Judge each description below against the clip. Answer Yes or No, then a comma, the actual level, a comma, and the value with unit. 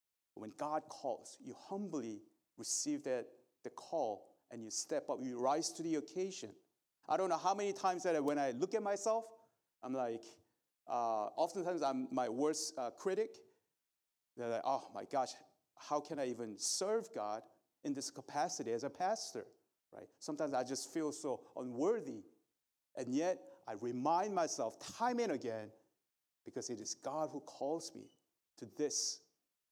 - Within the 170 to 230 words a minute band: No, average, 160 wpm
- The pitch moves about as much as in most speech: No, wide, 8.2 semitones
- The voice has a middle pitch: Yes, medium, 155 Hz